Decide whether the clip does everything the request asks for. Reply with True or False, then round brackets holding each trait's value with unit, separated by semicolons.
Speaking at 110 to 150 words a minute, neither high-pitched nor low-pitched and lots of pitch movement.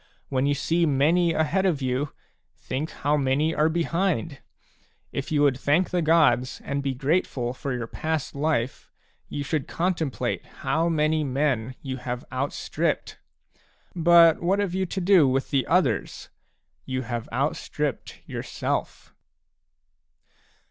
False (140 wpm; 145 Hz; 3.9 semitones)